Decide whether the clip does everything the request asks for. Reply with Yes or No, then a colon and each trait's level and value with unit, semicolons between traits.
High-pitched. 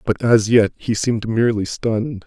No: low, 110 Hz